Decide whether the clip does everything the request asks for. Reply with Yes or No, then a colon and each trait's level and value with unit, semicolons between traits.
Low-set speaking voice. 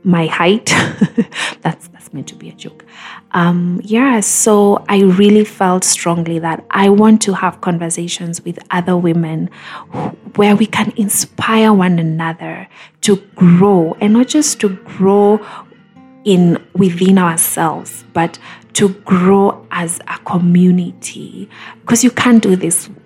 No: high, 190 Hz